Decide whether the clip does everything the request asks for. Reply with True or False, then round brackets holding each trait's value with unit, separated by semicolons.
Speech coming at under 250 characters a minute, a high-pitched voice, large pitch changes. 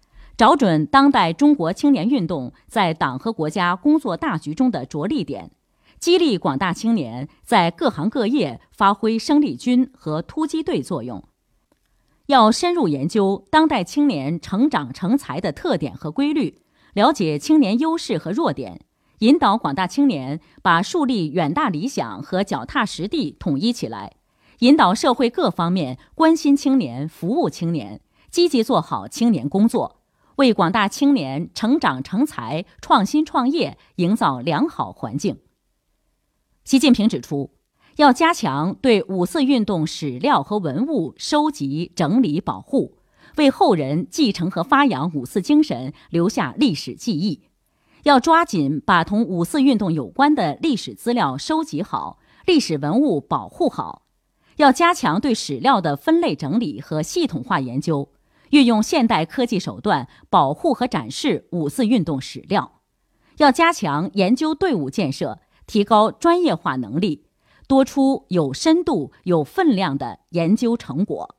True (230 characters per minute; 230 Hz; 8.9 semitones)